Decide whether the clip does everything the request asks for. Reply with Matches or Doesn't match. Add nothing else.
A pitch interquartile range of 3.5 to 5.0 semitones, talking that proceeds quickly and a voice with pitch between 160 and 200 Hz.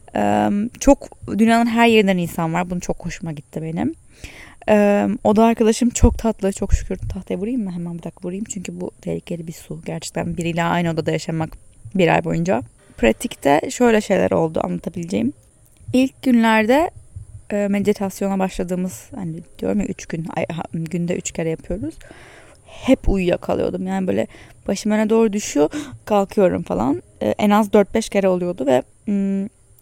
Matches